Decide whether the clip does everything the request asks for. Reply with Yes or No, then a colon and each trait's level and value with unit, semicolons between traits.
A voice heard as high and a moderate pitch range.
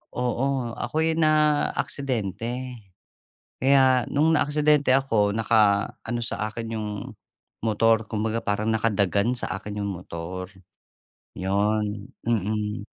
No: low, 115 Hz; average, 3.8 semitones